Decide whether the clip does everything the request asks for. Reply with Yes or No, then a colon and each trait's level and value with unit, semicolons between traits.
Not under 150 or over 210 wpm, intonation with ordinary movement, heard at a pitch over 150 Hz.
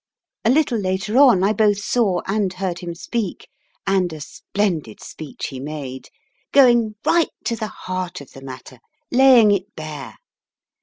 No: average, 155 wpm; wide, 5.8 semitones; high, 190 Hz